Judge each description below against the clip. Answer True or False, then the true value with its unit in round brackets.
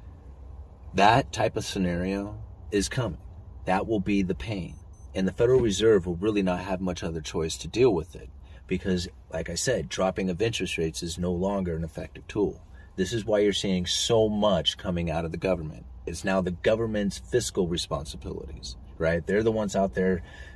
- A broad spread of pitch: False (3.0 semitones)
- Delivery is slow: False (185 wpm)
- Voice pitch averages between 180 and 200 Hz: False (90 Hz)